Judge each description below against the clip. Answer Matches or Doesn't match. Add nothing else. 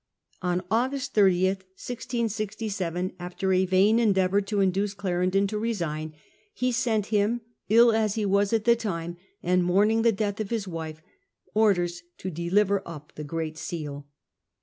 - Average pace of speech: Matches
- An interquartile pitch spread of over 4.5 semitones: Doesn't match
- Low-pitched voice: Doesn't match